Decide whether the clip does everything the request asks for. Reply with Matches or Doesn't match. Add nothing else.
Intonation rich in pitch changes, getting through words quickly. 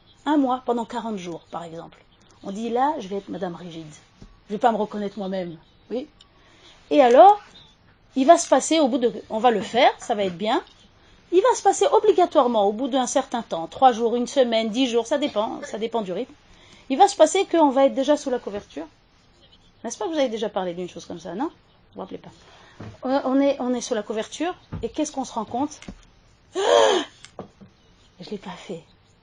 Matches